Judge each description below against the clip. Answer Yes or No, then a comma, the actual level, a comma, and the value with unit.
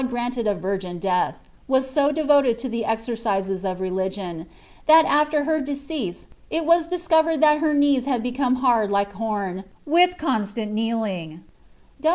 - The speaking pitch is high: Yes, high, 240 Hz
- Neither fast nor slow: Yes, average, 150 wpm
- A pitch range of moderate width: No, wide, 6.6 semitones